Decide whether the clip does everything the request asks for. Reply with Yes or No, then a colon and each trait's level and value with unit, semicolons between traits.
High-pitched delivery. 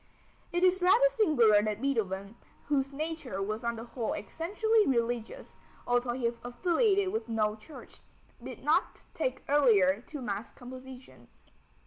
Yes: very high, 250 Hz